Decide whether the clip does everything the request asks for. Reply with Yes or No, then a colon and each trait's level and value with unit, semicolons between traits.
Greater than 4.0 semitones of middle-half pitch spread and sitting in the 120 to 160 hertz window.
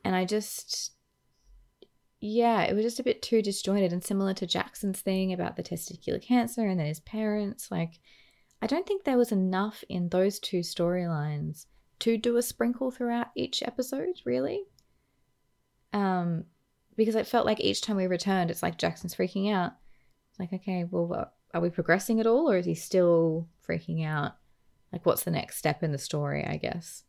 No: average, 4.6 semitones; high, 190 Hz